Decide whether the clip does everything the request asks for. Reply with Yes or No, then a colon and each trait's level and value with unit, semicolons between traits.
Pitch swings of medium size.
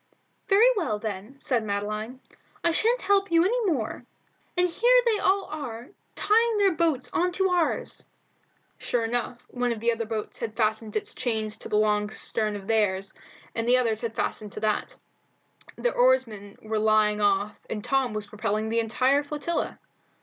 No: wide, 7.9 semitones